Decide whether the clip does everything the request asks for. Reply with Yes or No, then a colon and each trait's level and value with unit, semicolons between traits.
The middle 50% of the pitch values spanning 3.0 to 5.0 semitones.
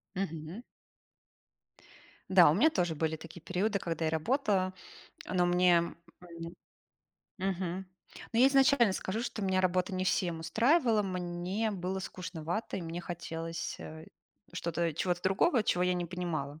No: narrow, 2.6 semitones